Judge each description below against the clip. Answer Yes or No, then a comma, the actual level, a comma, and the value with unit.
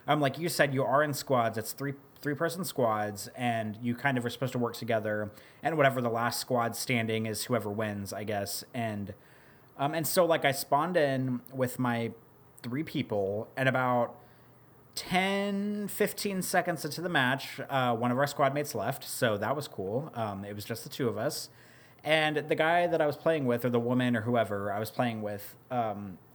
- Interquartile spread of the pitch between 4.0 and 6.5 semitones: Yes, average, 4.3 semitones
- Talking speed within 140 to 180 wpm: No, fast, 205 wpm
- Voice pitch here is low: Yes, low, 125 Hz